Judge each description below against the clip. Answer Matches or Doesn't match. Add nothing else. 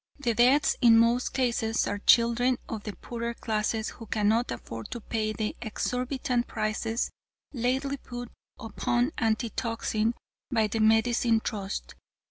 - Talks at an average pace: Doesn't match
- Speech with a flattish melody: Matches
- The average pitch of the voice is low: Doesn't match